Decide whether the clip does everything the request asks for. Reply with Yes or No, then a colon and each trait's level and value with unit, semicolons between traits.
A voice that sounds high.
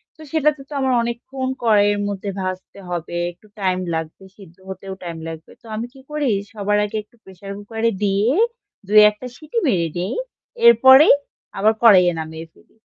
Yes: high, 205 Hz